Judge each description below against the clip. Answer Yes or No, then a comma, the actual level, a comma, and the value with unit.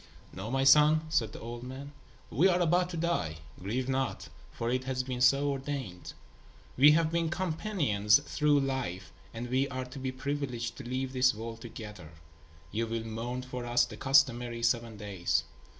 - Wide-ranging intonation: No, average, 3.4 semitones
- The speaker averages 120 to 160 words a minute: No, average, 175 wpm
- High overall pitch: No, low, 130 Hz